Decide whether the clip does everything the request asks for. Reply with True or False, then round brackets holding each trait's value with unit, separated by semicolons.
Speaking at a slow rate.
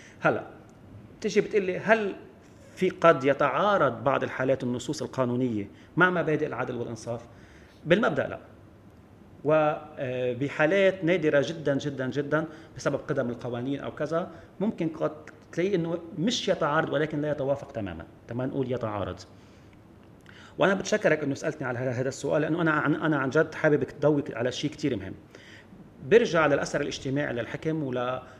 True (130 wpm)